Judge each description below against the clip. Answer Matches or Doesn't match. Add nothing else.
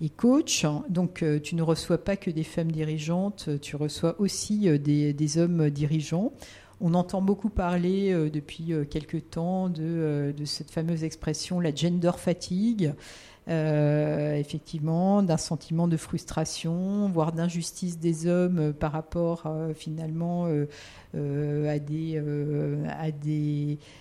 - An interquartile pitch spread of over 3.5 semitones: Doesn't match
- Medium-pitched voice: Matches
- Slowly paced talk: Matches